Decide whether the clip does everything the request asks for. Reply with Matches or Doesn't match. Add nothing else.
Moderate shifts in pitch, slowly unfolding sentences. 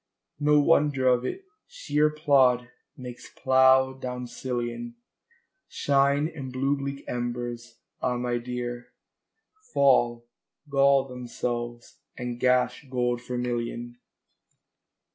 Doesn't match